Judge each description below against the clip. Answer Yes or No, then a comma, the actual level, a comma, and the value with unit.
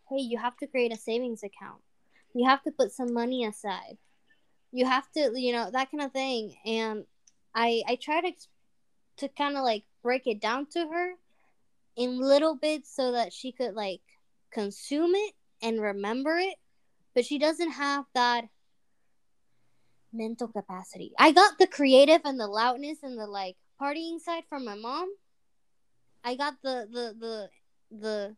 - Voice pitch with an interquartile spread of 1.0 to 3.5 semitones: No, average, 4.2 semitones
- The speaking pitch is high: Yes, very high, 250 Hz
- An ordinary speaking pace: Yes, average, 165 wpm